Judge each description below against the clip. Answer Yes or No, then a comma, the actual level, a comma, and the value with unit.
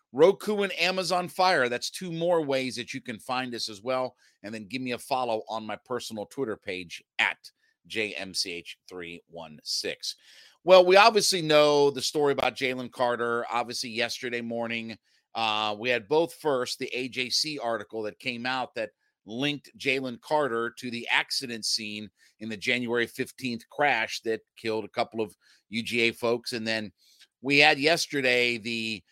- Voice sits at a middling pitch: No, low, 120 Hz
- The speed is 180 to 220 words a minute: No, average, 160 wpm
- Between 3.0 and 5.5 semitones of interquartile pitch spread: Yes, average, 4.1 semitones